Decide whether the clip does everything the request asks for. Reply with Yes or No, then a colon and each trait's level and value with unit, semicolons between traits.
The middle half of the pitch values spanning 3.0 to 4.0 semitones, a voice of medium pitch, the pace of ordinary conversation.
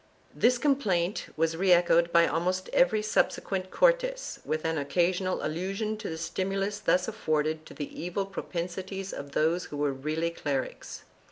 Yes: average, 3.4 semitones; medium, 180 Hz; average, 160 wpm